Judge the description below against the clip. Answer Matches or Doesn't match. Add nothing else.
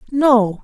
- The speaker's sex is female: Matches